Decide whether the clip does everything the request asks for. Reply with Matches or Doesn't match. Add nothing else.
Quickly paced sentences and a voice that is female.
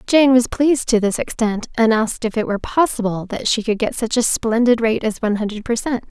Matches